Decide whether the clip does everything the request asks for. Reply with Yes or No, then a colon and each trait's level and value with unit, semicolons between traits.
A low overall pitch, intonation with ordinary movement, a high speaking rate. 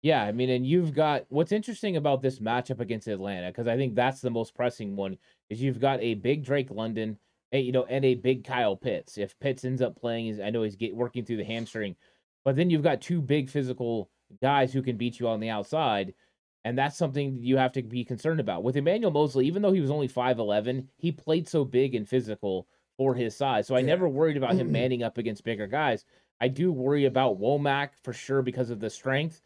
Yes: low, 130 Hz; average, 3.4 semitones; fast, 230 wpm